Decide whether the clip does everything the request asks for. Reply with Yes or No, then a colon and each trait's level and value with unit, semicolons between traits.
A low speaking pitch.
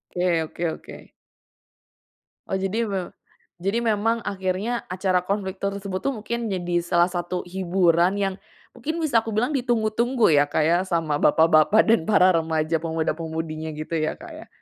No: medium, 185 Hz